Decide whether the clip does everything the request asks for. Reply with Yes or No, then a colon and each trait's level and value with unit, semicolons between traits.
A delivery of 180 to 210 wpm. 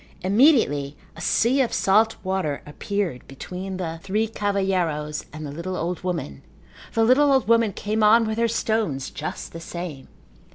No: average, 160 wpm